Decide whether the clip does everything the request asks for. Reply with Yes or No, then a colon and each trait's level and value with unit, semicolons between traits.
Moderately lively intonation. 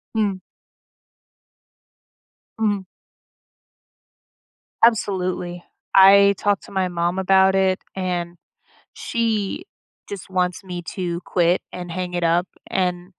No: narrow, 1.8 semitones